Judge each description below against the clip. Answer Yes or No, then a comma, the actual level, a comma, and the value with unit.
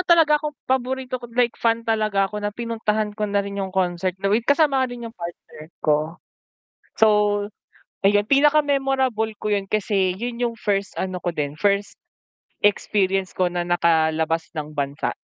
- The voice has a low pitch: No, high, 205 Hz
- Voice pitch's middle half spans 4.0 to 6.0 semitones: Yes, average, 4.6 semitones